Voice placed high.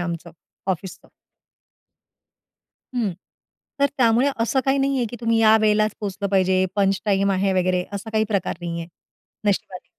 Yes: high, 200 Hz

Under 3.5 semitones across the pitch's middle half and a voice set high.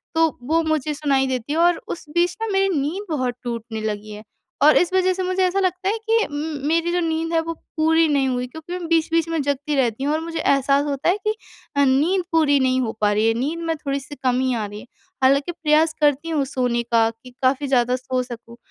No: average, 4.4 semitones; very high, 290 Hz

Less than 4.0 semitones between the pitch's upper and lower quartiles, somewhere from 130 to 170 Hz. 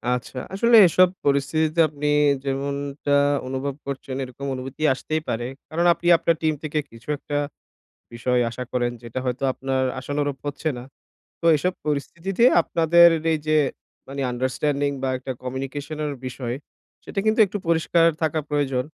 Yes: average, 3.3 semitones; medium, 140 Hz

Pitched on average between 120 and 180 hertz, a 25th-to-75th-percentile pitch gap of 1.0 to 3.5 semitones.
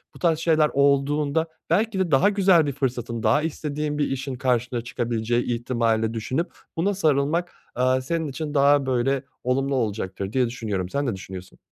No: low, 135 Hz; average, 4.1 semitones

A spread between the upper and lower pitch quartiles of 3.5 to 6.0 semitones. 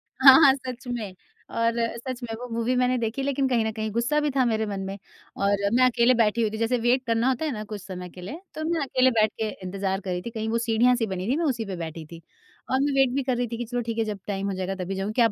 Yes: average, 3.9 semitones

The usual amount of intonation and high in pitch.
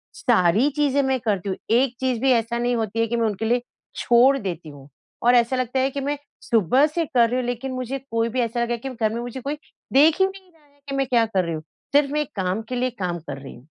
Yes: average, 3.4 semitones; high, 240 Hz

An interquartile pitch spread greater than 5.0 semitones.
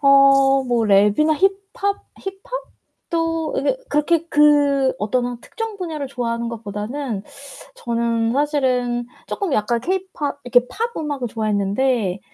Yes: wide, 5.4 semitones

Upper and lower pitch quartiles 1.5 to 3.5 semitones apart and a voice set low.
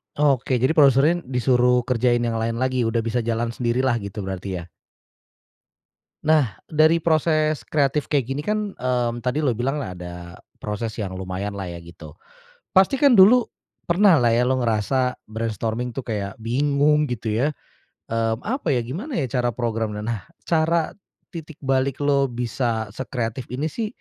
No: average, 4.6 semitones; low, 125 Hz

